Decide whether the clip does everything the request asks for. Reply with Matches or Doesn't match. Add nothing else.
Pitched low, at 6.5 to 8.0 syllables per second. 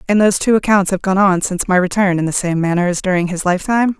Doesn't match